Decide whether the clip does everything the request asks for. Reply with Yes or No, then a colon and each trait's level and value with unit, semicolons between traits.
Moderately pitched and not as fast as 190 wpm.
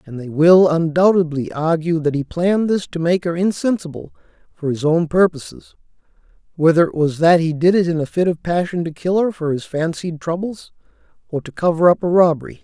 No: medium, 170 Hz; average, 200 wpm